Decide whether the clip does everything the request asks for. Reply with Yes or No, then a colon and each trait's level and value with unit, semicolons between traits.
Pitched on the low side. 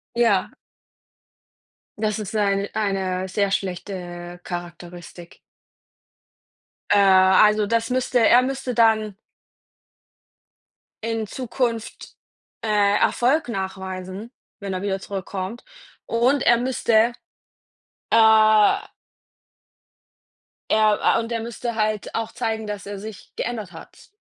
No: high, 210 Hz